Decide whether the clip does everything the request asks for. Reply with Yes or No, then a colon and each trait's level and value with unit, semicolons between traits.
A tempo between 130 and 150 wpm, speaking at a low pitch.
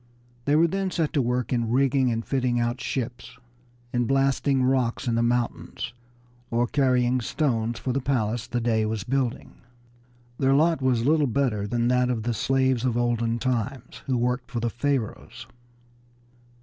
No: average, 170 wpm; low, 125 Hz